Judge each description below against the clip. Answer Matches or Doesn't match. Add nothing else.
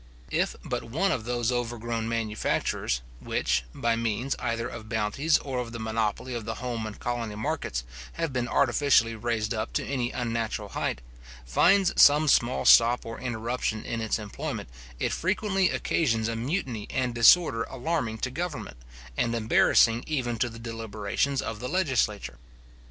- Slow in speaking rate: Doesn't match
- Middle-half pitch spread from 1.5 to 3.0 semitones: Matches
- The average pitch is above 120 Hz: Doesn't match